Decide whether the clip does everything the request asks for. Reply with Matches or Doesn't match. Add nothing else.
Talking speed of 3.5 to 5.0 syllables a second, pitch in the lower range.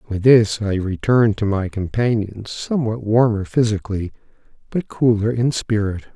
Matches